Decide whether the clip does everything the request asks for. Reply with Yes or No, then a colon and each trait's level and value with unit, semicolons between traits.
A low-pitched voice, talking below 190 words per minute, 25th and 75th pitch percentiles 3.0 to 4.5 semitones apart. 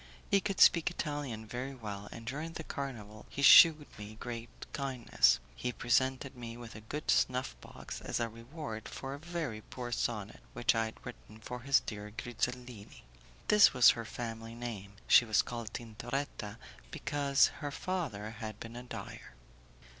Yes: low, 120 Hz; average, 160 wpm; average, 3.9 semitones